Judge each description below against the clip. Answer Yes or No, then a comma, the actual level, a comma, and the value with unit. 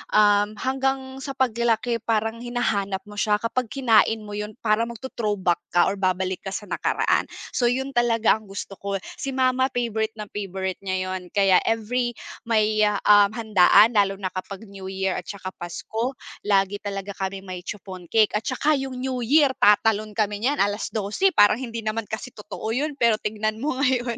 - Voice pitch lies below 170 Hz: No, high, 215 Hz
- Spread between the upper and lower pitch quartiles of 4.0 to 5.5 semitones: No, average, 3.2 semitones